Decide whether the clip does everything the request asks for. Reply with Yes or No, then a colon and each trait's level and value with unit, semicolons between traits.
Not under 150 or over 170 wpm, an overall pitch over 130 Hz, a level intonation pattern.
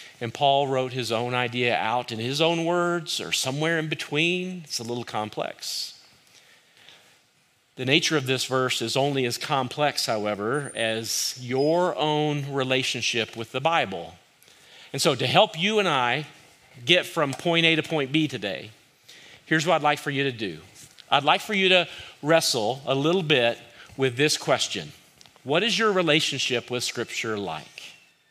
No: average, 165 wpm; medium, 140 Hz; average, 4.7 semitones